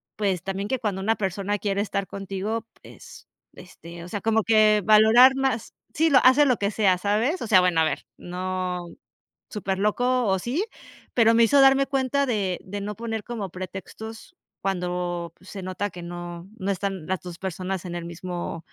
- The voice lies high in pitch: Yes, high, 200 Hz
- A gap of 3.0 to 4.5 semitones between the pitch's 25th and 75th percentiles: Yes, average, 3.6 semitones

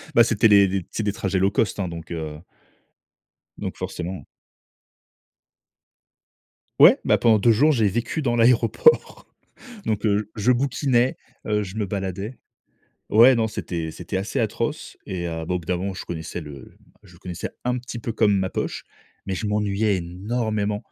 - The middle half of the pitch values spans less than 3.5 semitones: No, average, 3.8 semitones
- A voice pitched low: Yes, low, 100 Hz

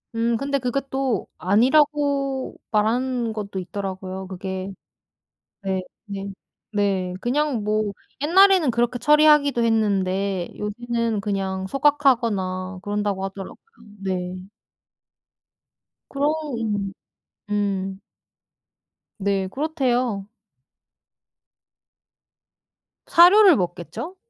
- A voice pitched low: No, high, 215 Hz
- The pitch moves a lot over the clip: Yes, wide, 5.7 semitones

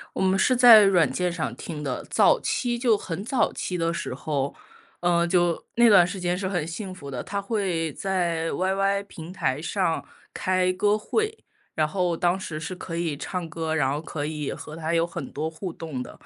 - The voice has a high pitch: No, medium, 175 Hz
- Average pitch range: Yes, average, 3.2 semitones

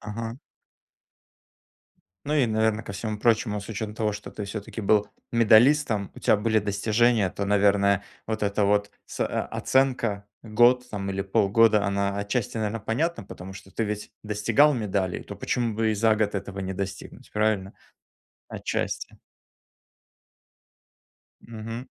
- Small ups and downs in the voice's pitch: Yes, narrow, 2.1 semitones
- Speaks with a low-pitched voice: Yes, low, 105 Hz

